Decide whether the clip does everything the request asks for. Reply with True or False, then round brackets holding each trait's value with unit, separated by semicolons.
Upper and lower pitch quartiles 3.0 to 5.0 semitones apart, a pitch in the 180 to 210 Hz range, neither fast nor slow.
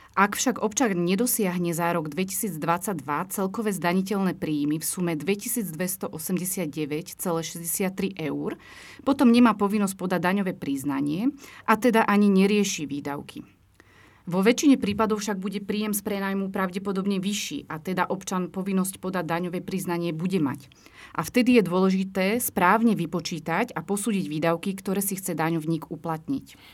True (3.5 semitones; 190 Hz; 130 wpm)